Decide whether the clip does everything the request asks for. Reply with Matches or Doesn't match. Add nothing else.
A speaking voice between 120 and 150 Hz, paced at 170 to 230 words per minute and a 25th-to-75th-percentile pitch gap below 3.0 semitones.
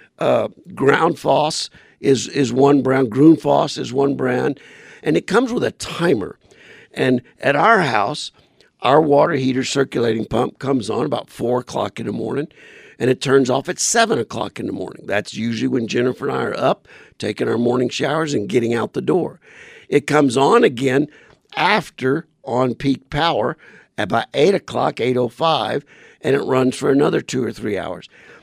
Matches